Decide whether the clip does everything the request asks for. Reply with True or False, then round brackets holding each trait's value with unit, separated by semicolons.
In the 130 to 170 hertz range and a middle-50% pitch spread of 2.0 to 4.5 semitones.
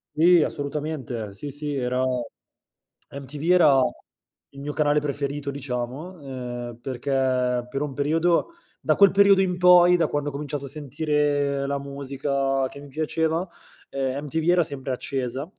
True (140 Hz; 2.7 semitones)